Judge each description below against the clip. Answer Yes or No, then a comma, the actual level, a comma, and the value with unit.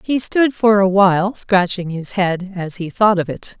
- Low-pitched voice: No, high, 195 Hz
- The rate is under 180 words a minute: No, average, 200 wpm